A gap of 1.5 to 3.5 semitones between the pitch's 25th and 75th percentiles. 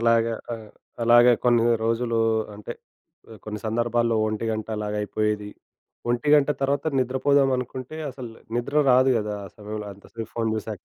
Yes: average, 2.8 semitones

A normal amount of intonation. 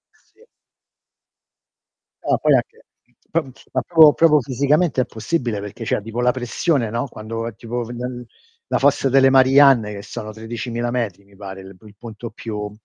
Yes: average, 3.9 semitones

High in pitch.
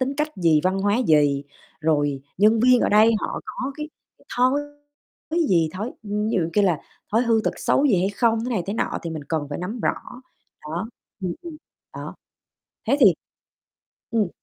Yes: high, 205 Hz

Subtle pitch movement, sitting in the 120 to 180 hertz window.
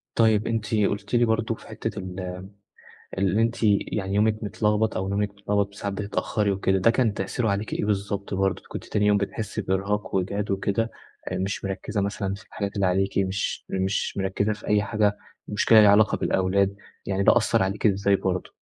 No: narrow, 1.5 semitones; low, 100 Hz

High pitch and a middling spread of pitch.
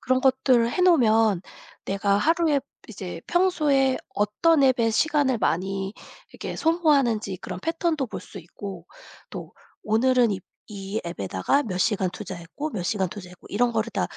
No: high, 225 Hz; wide, 6.2 semitones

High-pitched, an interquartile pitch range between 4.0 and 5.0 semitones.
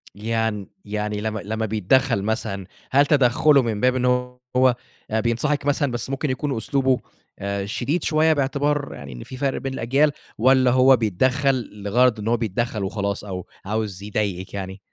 No: low, 115 Hz; average, 4.3 semitones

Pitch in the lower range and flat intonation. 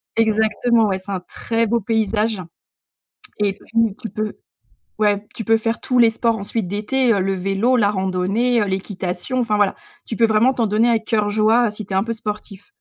No: high, 215 Hz; narrow, 2.3 semitones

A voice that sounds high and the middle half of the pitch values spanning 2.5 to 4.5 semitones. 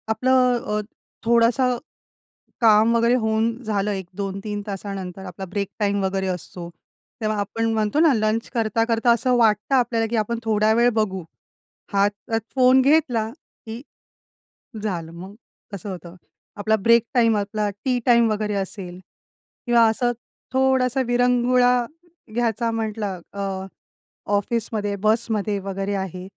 Yes: high, 220 Hz; average, 2.9 semitones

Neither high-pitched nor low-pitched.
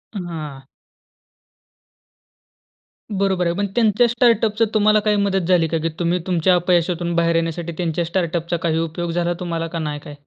Yes: medium, 175 Hz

